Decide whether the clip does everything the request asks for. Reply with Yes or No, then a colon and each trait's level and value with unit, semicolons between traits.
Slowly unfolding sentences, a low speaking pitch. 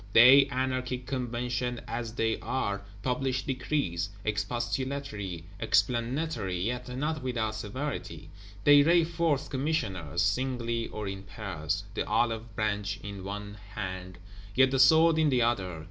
Yes: slow, 130 wpm; low, 120 Hz